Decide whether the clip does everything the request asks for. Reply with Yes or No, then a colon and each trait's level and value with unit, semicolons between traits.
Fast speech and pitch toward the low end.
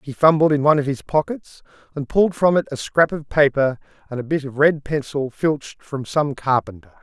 No: fast, 215 wpm; medium, 145 Hz